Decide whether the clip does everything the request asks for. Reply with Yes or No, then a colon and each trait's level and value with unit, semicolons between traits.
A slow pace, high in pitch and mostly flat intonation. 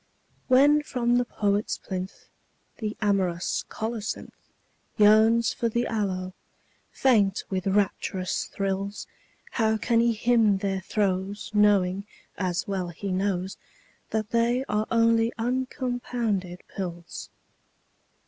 No: slow, 110 wpm; high, 210 Hz; average, 3.4 semitones